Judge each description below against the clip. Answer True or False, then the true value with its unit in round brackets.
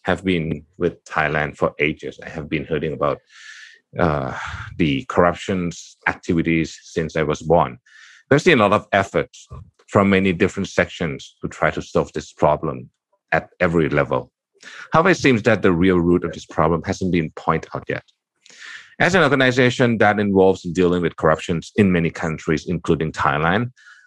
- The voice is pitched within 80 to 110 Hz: True (90 Hz)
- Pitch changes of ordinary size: True (3.4 semitones)